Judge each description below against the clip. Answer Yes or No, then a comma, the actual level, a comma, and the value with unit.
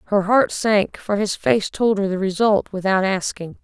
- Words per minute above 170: Yes, average, 200 wpm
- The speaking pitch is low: No, high, 200 Hz